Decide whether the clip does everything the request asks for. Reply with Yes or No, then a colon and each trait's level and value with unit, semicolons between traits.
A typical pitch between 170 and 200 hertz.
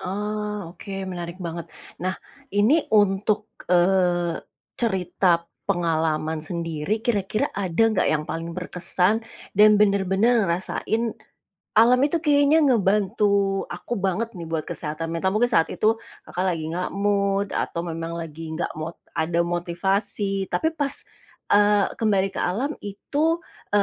Yes: high, 190 Hz